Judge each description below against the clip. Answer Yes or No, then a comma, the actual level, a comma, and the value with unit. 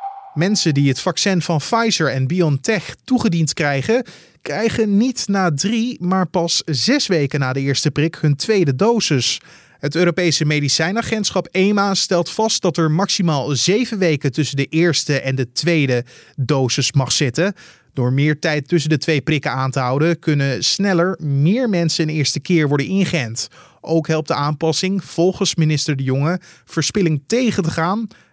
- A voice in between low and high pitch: Yes, medium, 165 Hz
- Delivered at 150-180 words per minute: Yes, average, 160 wpm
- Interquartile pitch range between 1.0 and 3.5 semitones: No, average, 4.6 semitones